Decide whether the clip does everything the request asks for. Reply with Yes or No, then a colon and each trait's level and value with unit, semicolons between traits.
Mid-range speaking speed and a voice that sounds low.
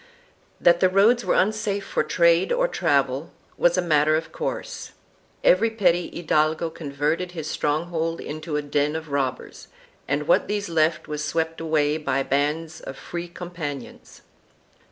No: average, 155 wpm; medium, 160 Hz